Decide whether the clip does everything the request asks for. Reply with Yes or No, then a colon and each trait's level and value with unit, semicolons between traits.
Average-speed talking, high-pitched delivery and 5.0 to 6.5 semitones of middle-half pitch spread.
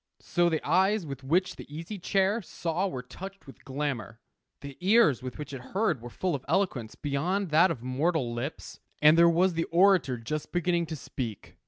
No: average, 190 wpm; medium, 160 Hz; wide, 5.4 semitones